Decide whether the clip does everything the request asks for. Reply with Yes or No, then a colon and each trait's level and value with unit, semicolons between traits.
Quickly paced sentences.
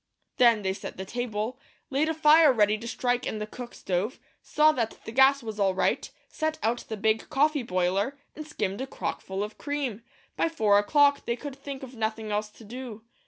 Yes: fast, 210 wpm